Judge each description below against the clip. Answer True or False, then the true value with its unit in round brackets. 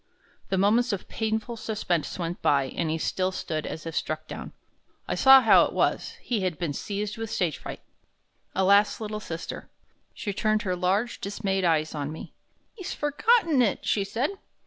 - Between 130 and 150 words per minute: False (175 wpm)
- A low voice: False (200 Hz)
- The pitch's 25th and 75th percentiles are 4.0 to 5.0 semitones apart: True (4.7 semitones)